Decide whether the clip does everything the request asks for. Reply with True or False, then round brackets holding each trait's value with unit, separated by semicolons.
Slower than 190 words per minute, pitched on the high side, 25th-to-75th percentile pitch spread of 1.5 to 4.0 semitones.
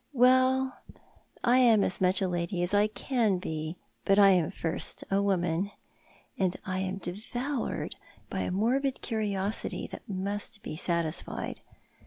False (145 wpm; 200 Hz; 4.5 semitones)